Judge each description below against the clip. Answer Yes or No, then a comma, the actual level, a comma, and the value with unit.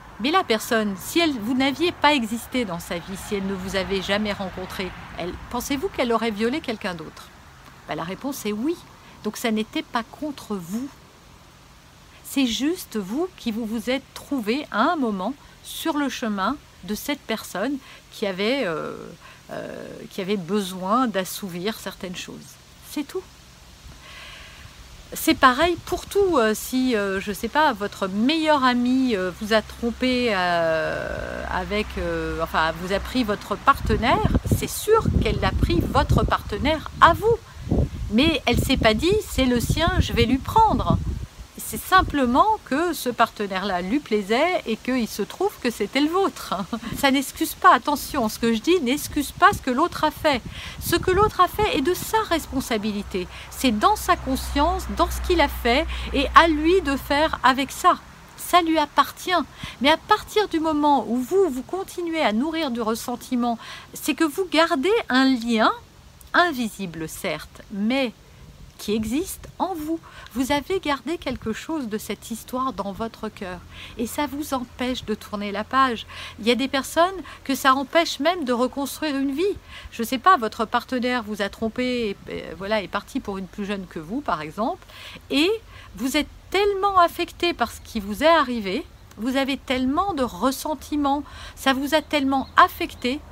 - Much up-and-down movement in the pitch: Yes, wide, 6.1 semitones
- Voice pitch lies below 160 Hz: No, very high, 260 Hz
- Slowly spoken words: No, average, 175 wpm